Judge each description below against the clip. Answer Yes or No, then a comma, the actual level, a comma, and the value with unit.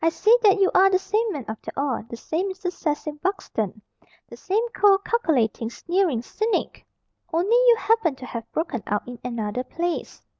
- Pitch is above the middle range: Yes, very high, 335 Hz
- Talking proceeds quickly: No, average, 180 wpm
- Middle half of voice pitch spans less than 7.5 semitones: No, wide, 8.3 semitones